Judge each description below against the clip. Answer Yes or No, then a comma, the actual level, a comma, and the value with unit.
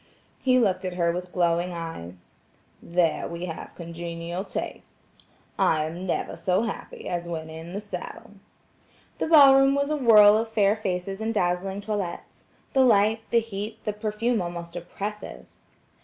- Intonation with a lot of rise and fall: No, average, 4.2 semitones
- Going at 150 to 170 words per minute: Yes, average, 155 wpm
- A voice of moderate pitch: No, high, 195 Hz